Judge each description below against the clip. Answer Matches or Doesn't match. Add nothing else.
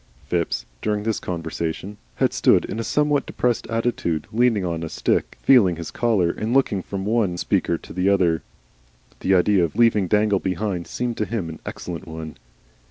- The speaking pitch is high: Doesn't match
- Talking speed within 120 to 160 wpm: Doesn't match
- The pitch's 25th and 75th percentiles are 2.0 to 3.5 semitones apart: Doesn't match